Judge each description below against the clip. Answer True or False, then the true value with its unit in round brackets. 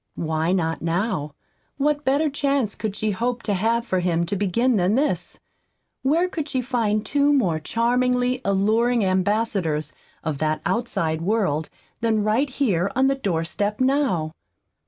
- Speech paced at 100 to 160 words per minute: True (155 wpm)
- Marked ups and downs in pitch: True (6.2 semitones)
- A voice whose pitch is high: True (215 Hz)